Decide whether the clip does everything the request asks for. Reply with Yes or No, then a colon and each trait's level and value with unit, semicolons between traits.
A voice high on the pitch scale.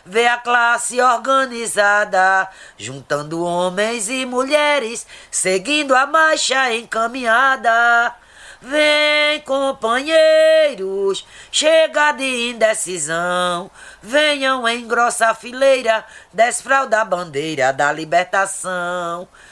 Yes: high, 235 Hz